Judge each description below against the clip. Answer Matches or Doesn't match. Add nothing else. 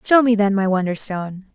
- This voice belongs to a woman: Matches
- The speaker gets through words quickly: Doesn't match